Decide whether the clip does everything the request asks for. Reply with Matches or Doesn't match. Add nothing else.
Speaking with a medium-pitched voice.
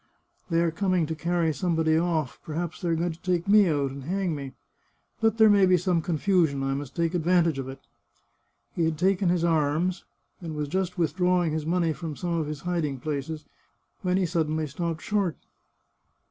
Matches